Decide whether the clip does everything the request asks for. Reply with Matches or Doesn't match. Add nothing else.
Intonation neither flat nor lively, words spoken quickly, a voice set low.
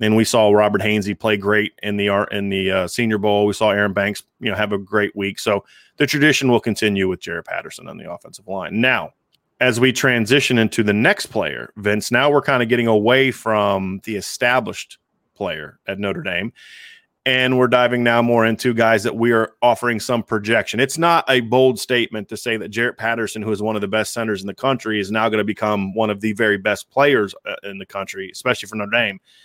Matches